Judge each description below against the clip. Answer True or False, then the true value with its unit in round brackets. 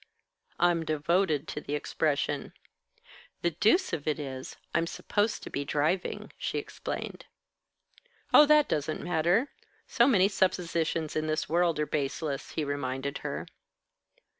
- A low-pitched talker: False (160 Hz)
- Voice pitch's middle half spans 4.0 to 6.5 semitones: False (3.6 semitones)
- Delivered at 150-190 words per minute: False (135 wpm)